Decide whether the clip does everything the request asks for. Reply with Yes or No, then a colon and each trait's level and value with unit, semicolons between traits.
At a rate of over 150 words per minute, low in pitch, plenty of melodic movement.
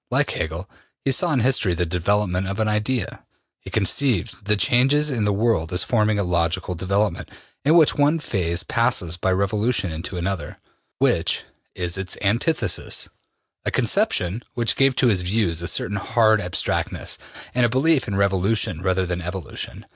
No: average, 165 wpm; low, 100 Hz; average, 4.7 semitones